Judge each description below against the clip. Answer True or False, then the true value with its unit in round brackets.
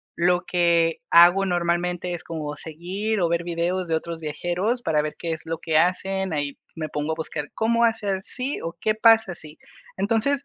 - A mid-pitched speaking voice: True (175 Hz)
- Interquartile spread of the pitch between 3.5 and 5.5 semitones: False (3.1 semitones)